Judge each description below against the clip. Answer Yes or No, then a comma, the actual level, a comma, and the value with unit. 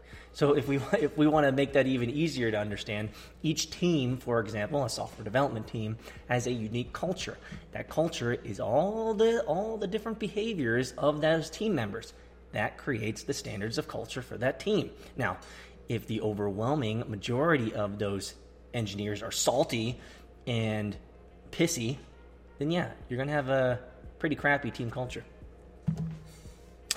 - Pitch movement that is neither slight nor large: No, wide, 5.9 semitones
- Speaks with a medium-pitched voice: No, low, 125 Hz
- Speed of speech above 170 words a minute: No, average, 155 wpm